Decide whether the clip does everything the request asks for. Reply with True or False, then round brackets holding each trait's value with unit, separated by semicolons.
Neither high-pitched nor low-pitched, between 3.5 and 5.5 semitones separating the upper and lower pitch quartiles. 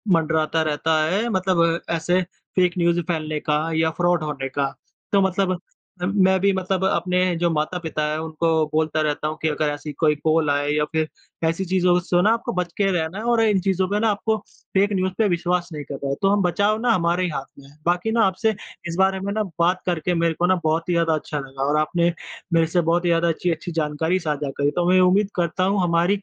False (175 Hz; 3.1 semitones)